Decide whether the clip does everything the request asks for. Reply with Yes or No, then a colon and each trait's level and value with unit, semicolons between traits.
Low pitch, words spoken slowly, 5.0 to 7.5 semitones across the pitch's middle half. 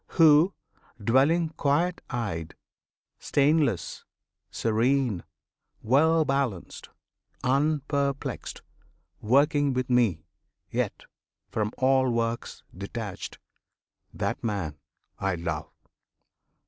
Yes: low, 130 Hz; slow, 75 wpm; wide, 5.4 semitones